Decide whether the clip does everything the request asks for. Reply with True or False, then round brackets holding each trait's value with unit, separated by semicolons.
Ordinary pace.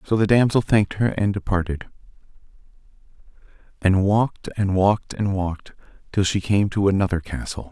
True (150 wpm)